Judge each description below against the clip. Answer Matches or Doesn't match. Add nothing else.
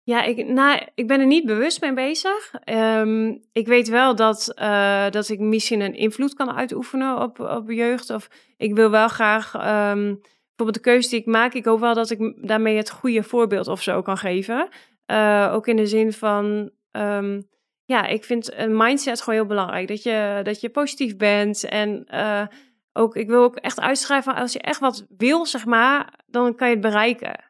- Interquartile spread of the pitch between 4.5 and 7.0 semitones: Doesn't match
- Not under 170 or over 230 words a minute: Matches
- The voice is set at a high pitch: Matches